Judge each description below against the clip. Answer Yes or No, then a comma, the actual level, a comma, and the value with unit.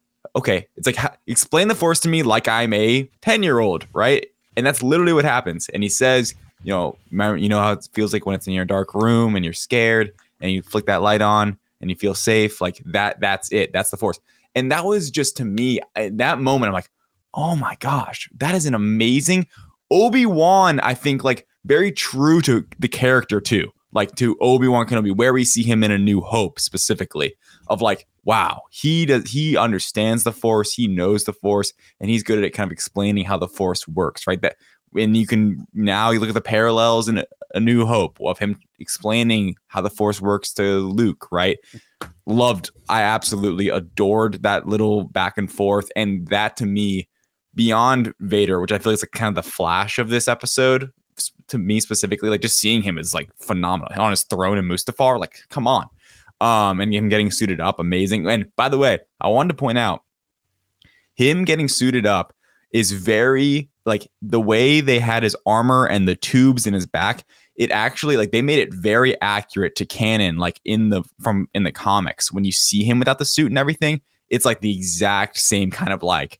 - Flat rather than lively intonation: No, average, 4.0 semitones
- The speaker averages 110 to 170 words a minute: No, fast, 205 wpm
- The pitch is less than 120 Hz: Yes, low, 110 Hz